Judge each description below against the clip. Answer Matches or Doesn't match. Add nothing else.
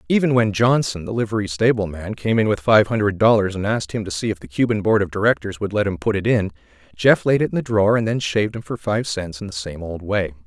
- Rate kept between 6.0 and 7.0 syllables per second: Matches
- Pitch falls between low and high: Doesn't match